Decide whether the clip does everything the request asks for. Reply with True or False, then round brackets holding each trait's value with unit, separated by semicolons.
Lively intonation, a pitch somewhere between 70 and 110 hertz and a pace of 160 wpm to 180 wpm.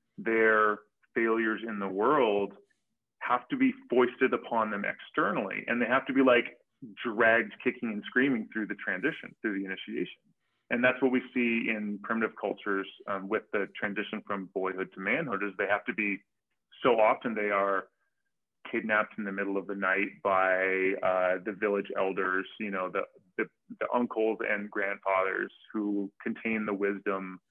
False (2.5 semitones; 105 Hz; 170 wpm)